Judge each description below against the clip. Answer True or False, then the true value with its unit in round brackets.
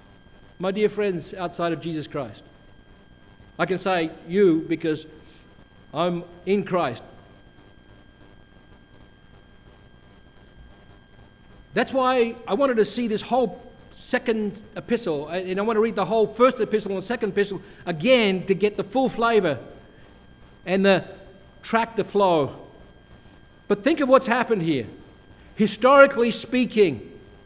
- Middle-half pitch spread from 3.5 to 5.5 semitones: True (4.8 semitones)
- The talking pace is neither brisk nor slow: False (120 wpm)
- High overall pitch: True (200 Hz)